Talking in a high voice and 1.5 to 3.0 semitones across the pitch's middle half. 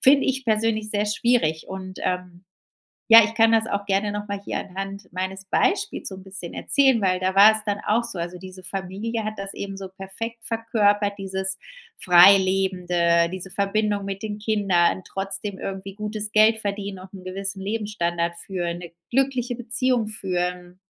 Yes: high, 195 Hz; narrow, 2.5 semitones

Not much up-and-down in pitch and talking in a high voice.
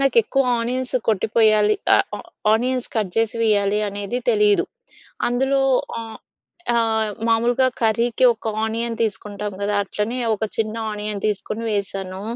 Yes: narrow, 2.2 semitones; high, 220 Hz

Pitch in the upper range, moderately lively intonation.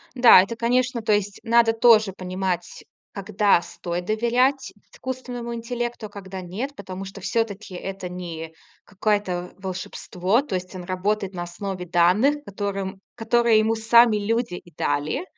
Yes: high, 205 Hz; average, 4.1 semitones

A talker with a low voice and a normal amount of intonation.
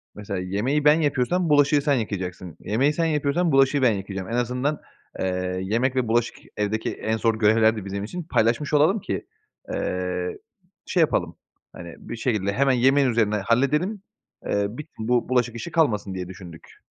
No: low, 115 Hz; wide, 6.0 semitones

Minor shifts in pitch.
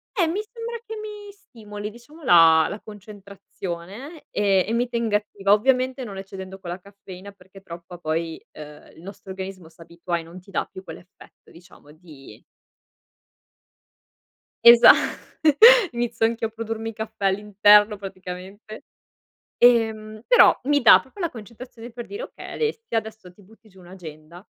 No: average, 4.3 semitones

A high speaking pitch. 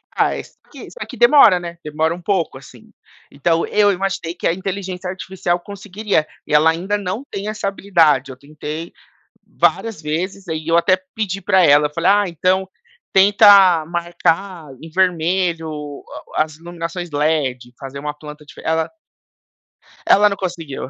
No: medium, 170 Hz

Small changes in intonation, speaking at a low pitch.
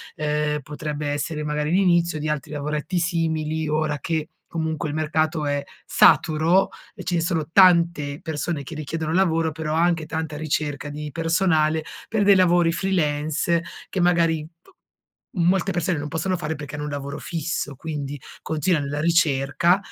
No: narrow, 2.2 semitones; medium, 160 Hz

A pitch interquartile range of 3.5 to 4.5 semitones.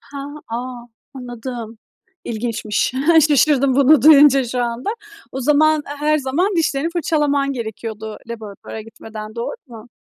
Yes: average, 4.1 semitones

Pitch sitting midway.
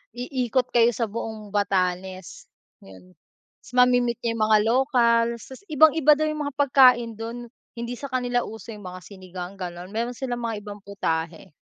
No: high, 230 Hz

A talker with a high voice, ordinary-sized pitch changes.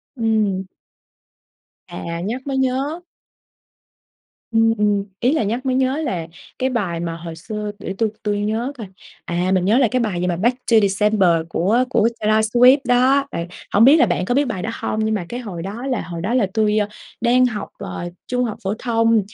Yes: high, 220 Hz; average, 4.3 semitones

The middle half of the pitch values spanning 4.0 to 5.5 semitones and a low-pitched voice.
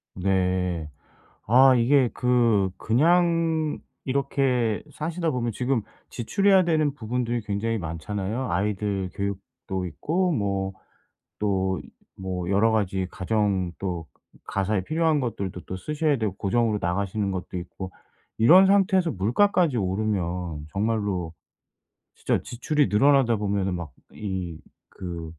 No: wide, 6.0 semitones; low, 105 Hz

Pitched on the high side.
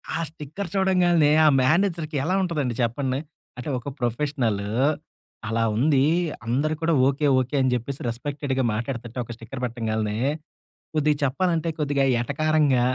No: medium, 140 Hz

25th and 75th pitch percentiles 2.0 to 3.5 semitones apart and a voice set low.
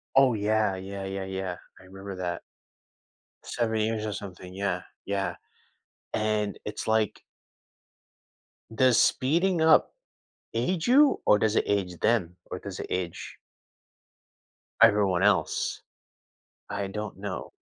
Yes: narrow, 2.6 semitones; low, 105 Hz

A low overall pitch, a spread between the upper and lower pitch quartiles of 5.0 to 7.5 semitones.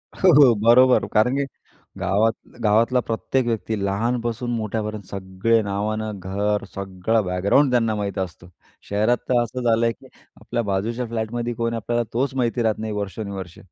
No: low, 110 Hz; average, 2.7 semitones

